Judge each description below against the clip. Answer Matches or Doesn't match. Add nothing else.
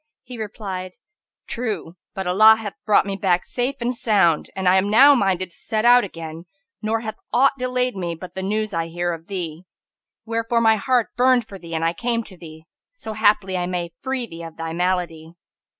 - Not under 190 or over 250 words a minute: Matches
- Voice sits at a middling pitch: Doesn't match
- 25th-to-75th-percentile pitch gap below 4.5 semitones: Doesn't match